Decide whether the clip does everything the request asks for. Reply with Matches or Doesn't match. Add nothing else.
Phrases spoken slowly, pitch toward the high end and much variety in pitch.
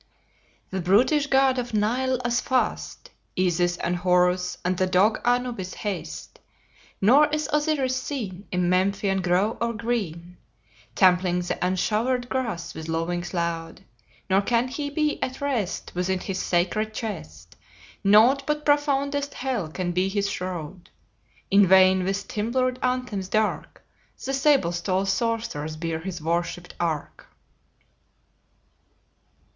Matches